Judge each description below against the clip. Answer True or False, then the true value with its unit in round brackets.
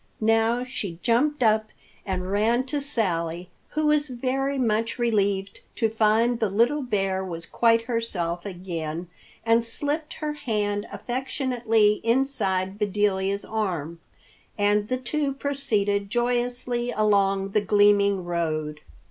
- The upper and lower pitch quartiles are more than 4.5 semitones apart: False (4.0 semitones)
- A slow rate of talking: True (125 wpm)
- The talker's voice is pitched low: False (215 Hz)